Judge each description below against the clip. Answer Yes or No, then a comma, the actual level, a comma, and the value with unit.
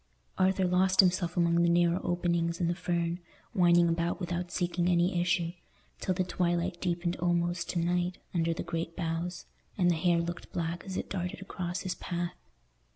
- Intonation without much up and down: Yes, narrow, 0.9 semitones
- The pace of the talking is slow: No, average, 175 wpm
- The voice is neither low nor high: Yes, medium, 175 Hz